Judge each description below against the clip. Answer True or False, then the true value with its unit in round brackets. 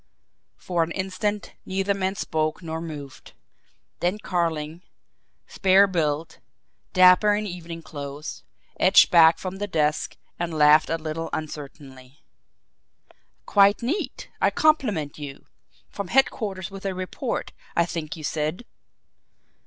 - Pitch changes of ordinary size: True (4.0 semitones)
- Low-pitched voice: False (170 Hz)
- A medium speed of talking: False (120 wpm)